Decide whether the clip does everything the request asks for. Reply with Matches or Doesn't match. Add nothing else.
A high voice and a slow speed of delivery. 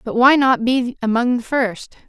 Doesn't match